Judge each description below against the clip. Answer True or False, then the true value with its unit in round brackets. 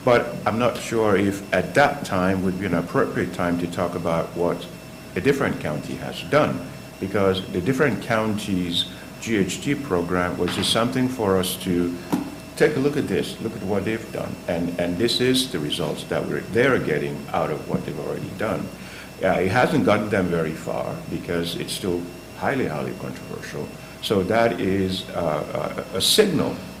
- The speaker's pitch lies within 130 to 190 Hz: False (90 Hz)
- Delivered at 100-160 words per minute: False (180 wpm)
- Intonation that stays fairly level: True (2.3 semitones)